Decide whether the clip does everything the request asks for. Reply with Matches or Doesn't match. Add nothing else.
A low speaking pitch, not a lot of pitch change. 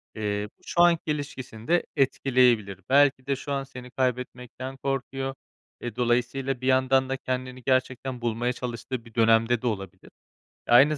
Matches